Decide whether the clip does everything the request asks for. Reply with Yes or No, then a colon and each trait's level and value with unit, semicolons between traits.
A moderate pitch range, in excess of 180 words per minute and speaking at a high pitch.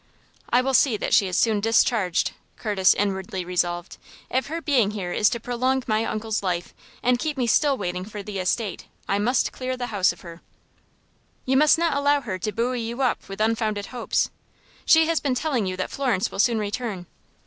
Yes: average, 4.7 semitones; average, 200 wpm; high, 225 Hz